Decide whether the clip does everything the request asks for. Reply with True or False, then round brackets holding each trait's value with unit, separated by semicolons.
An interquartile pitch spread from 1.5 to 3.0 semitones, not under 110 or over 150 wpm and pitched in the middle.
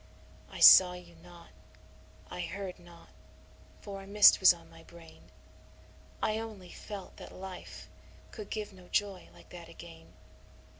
True (2.7 semitones; 145 wpm; 180 Hz)